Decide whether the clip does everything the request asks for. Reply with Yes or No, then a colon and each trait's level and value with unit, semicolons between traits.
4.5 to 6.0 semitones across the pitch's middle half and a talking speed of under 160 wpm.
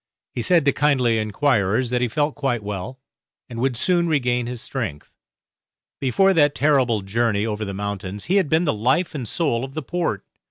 No: average, 5.0 semitones; average, 190 wpm